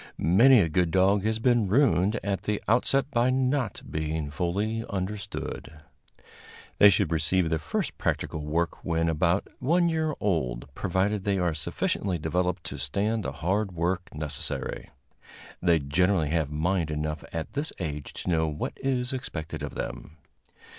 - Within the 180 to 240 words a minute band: No, average, 155 wpm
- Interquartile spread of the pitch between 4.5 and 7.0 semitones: Yes, average, 5.0 semitones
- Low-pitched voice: Yes, very low, 90 Hz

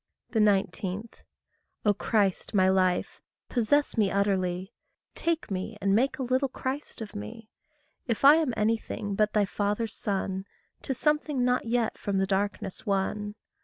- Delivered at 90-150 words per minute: Yes, average, 145 wpm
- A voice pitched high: Yes, high, 210 Hz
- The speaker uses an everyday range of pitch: Yes, average, 3.9 semitones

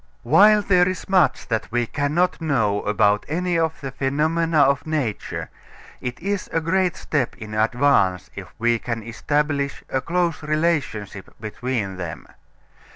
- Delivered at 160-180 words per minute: No, average, 145 wpm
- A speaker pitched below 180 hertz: Yes, medium, 140 Hz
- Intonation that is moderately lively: No, wide, 6.5 semitones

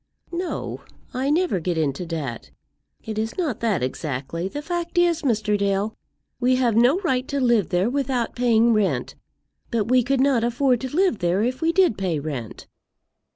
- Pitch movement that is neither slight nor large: No, wide, 6.4 semitones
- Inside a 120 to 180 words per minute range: Yes, average, 175 wpm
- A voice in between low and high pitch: No, high, 235 Hz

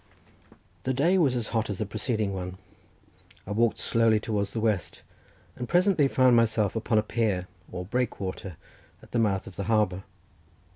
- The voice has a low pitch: Yes, low, 110 Hz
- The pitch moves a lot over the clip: No, average, 3.3 semitones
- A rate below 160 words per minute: No, average, 165 wpm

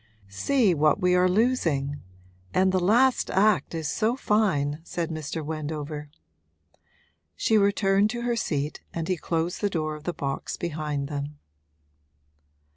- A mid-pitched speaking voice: Yes, medium, 170 Hz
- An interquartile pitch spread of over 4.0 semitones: Yes, average, 5.2 semitones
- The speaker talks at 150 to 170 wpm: No, average, 140 wpm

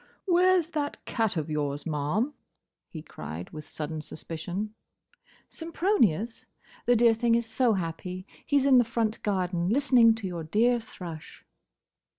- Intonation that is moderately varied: No, wide, 6.9 semitones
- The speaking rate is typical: Yes, average, 145 wpm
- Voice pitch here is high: Yes, high, 215 Hz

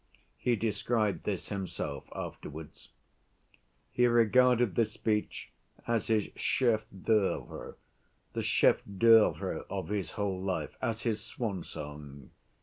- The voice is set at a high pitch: No, low, 105 Hz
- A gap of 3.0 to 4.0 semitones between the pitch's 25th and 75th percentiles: Yes, average, 3.4 semitones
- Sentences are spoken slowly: Yes, slow, 100 wpm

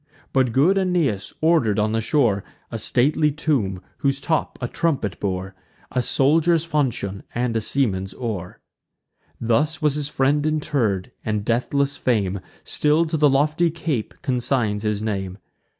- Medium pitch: No, low, 130 Hz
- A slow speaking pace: No, average, 145 wpm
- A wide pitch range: Yes, wide, 6.0 semitones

